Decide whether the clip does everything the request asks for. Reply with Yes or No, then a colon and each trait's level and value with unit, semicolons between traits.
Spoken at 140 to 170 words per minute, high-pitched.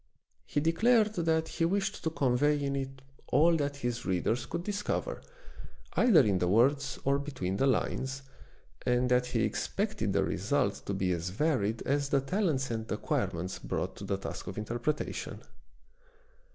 No: average, 160 wpm; low, 135 Hz